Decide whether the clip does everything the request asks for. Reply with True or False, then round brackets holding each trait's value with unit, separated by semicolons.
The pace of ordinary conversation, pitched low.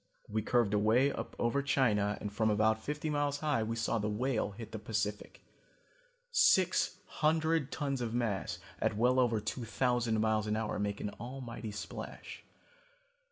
True (160 wpm; 115 Hz)